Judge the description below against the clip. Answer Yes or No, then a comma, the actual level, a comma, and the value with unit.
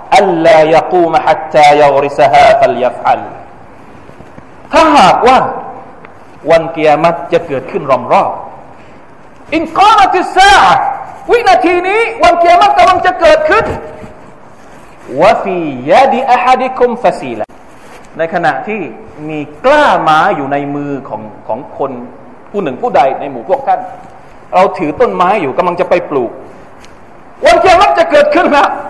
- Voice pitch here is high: Yes, very high, 275 Hz